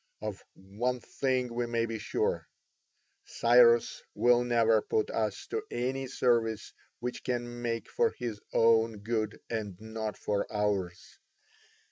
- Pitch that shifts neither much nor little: No, narrow, 2.3 semitones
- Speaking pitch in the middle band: No, low, 115 Hz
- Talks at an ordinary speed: No, slow, 130 wpm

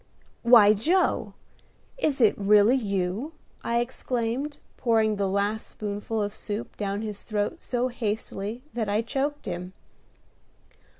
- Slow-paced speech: Yes, slow, 125 wpm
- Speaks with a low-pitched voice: No, high, 220 Hz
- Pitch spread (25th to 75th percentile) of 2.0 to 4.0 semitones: Yes, average, 3.1 semitones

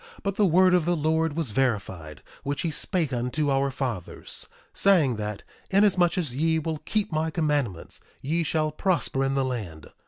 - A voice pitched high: No, medium, 150 Hz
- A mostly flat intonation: No, average, 4.8 semitones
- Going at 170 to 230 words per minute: Yes, average, 175 wpm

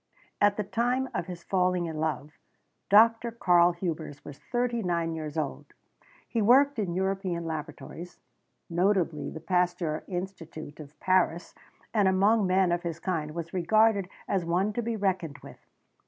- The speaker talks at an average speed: Yes, average, 155 wpm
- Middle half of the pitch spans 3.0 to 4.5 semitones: Yes, average, 3.5 semitones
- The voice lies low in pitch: No, medium, 180 Hz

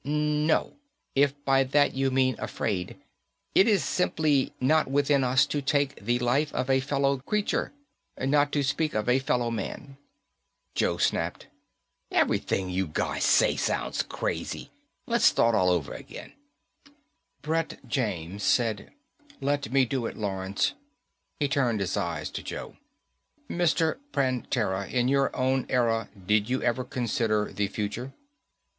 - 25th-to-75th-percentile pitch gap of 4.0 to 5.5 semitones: Yes, average, 4.3 semitones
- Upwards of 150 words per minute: No, average, 140 wpm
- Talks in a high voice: No, low, 130 Hz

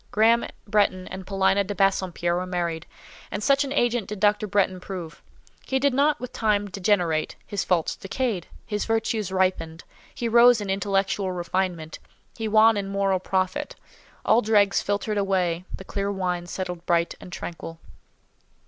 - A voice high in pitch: Yes, high, 195 Hz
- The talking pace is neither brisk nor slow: Yes, average, 155 wpm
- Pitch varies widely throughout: No, average, 2.8 semitones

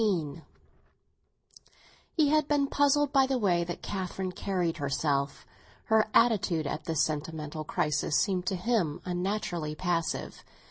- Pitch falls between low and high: Yes, medium, 180 Hz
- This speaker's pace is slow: Yes, slow, 130 wpm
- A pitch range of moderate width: No, wide, 6.0 semitones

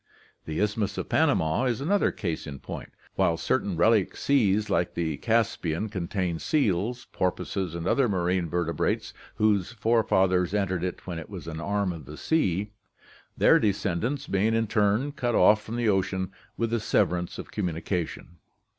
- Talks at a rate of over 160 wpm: Yes, average, 170 wpm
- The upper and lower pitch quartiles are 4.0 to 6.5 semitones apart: Yes, average, 4.3 semitones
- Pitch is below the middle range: Yes, low, 100 Hz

